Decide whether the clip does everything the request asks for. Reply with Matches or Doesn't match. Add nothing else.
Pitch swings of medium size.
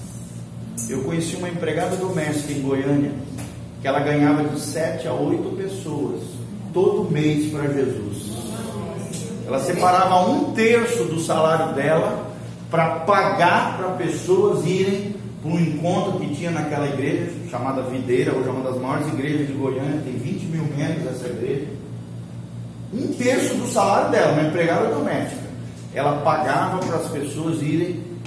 Matches